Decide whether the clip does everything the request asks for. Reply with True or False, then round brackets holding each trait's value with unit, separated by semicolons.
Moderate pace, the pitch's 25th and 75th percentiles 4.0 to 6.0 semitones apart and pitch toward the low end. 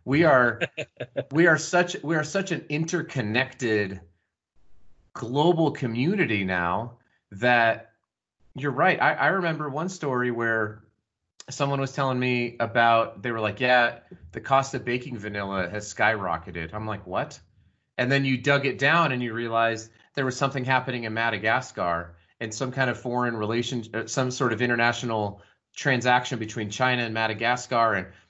False (155 wpm; 3.6 semitones; 120 Hz)